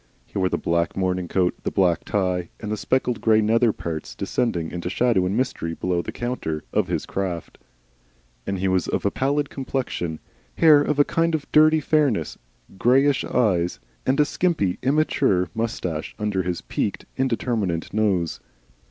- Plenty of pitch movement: Yes, wide, 6.6 semitones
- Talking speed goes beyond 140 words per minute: Yes, average, 160 wpm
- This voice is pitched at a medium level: No, low, 105 Hz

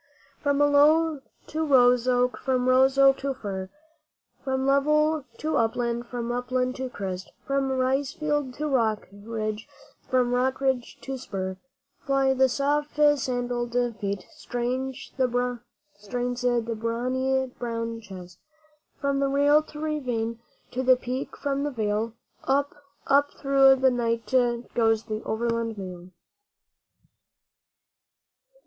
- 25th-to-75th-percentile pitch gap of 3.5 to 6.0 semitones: No, average, 2.9 semitones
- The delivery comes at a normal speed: No, slow, 120 wpm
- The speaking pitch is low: No, very high, 255 Hz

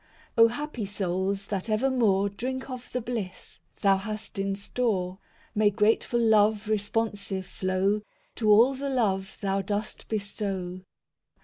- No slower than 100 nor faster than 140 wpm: Yes, slow, 135 wpm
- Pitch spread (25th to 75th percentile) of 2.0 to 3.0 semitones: Yes, average, 2.7 semitones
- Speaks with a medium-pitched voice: No, high, 210 Hz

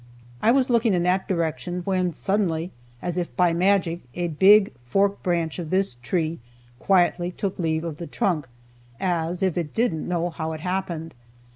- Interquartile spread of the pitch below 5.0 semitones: Yes, average, 2.7 semitones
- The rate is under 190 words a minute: Yes, average, 170 wpm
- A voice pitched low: No, medium, 175 Hz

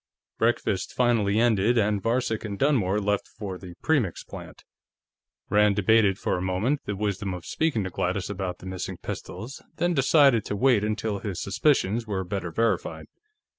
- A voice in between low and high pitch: No, low, 105 Hz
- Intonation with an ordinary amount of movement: Yes, average, 3.5 semitones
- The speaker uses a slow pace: No, average, 165 wpm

